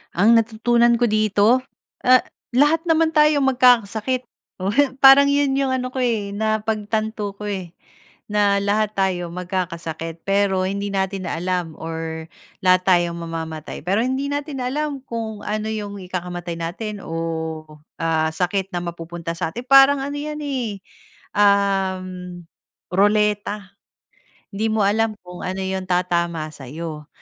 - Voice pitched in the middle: No, high, 200 Hz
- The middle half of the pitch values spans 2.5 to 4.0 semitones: No, average, 4.8 semitones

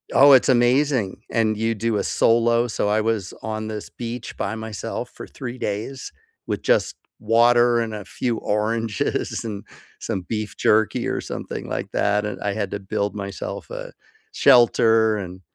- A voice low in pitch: Yes, low, 110 Hz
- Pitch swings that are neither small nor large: No, narrow, 2.1 semitones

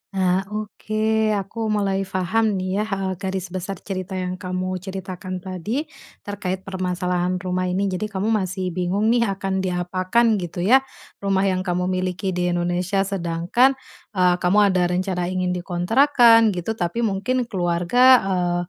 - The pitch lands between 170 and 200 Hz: Yes, medium, 185 Hz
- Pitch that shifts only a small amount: Yes, narrow, 1.8 semitones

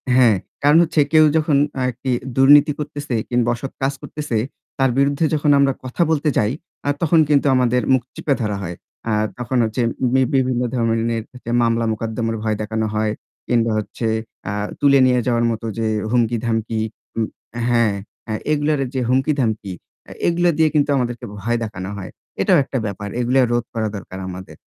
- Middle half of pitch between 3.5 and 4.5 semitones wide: Yes, average, 3.9 semitones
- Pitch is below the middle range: Yes, low, 125 Hz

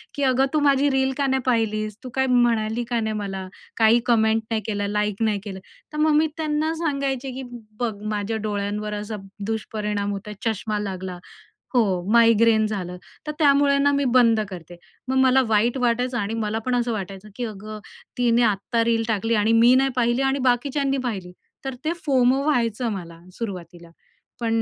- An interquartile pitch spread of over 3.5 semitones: Yes, average, 3.9 semitones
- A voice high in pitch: Yes, high, 230 Hz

